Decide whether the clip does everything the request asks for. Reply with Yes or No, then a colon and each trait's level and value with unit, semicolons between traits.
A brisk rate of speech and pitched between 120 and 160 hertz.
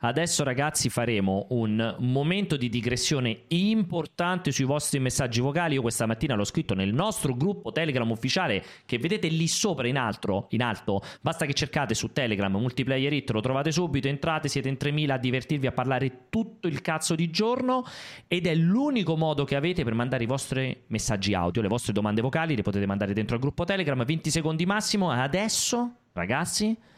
Yes: fast, 180 wpm; medium, 140 Hz